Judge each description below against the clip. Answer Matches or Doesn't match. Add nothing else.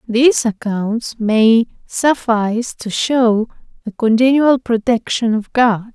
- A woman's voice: Matches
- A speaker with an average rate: Doesn't match